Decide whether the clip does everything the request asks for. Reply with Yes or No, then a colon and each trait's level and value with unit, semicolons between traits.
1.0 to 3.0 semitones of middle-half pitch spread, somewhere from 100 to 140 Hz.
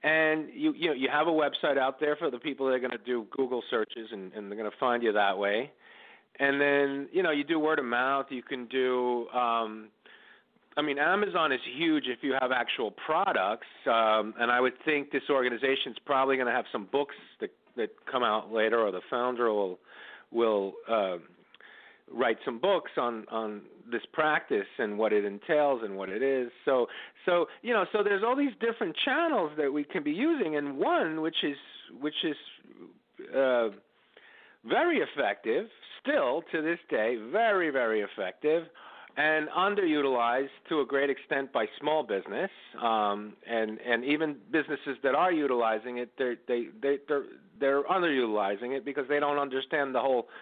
No: average, 4.0 semitones; low, 135 Hz